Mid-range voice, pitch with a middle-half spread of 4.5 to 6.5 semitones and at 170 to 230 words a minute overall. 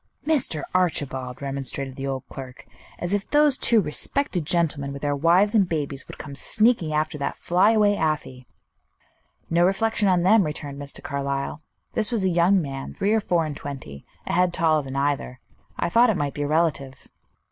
Yes: medium, 155 Hz; wide, 5.6 semitones; average, 180 wpm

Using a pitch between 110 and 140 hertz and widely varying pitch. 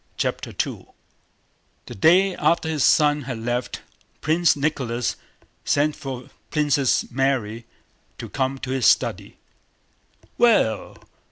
No: low, 135 Hz; average, 3.7 semitones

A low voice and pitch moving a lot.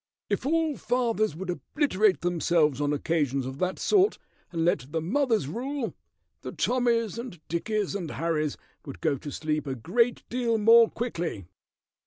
No: medium, 185 Hz; wide, 7.4 semitones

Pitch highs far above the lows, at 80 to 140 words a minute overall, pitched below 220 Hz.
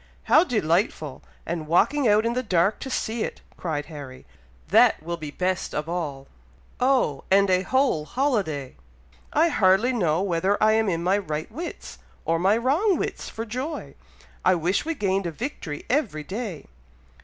No: wide, 6.8 semitones; average, 165 wpm; high, 190 Hz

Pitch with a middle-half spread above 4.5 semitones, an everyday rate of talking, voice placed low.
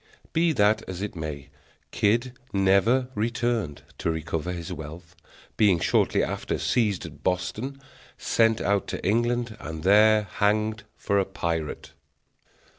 No: average, 4.9 semitones; slow, 130 wpm; low, 100 Hz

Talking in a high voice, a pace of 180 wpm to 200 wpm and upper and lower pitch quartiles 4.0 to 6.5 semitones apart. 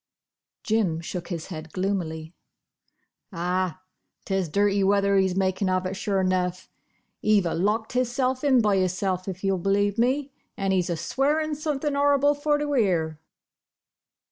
No: high, 195 Hz; average, 145 wpm; average, 5.3 semitones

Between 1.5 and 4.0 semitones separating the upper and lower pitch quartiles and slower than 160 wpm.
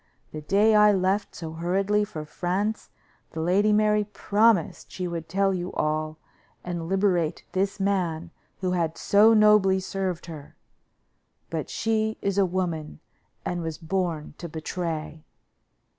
Yes: average, 3.7 semitones; average, 140 wpm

